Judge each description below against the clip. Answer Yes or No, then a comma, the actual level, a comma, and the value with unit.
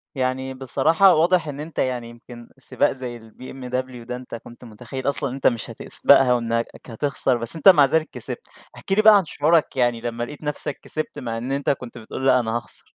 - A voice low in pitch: Yes, low, 130 Hz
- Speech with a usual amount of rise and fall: Yes, average, 3.6 semitones